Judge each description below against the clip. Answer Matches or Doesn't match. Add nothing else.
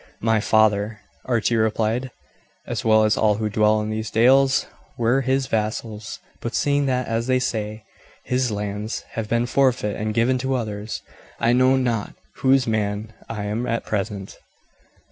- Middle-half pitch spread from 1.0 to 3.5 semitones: Matches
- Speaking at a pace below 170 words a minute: Matches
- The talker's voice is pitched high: Doesn't match